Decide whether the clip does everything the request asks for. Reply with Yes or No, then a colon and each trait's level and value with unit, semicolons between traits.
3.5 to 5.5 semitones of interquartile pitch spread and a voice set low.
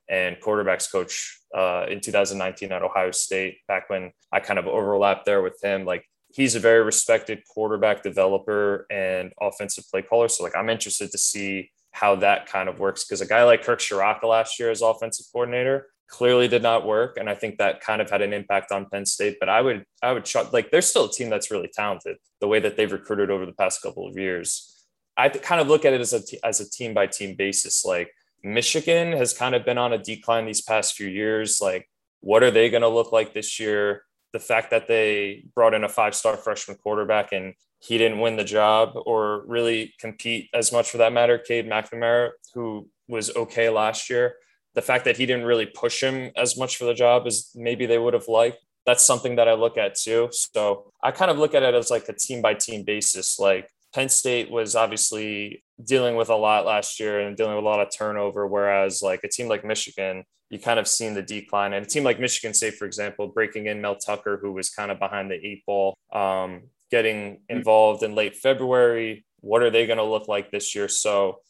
No: average, 2.8 semitones; low, 110 Hz